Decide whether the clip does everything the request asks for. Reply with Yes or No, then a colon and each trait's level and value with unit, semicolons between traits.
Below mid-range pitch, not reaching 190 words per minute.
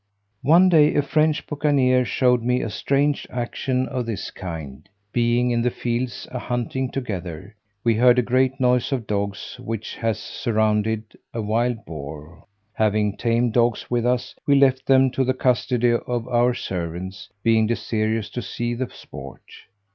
Yes: low, 120 Hz; average, 160 wpm